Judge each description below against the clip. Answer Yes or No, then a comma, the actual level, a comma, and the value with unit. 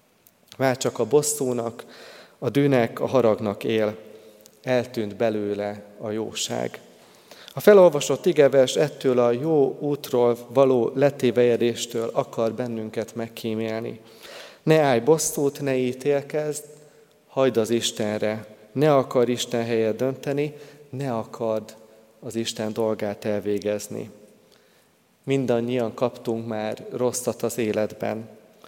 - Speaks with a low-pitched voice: Yes, low, 120 Hz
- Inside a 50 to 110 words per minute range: Yes, slow, 105 wpm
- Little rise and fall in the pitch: No, average, 3.8 semitones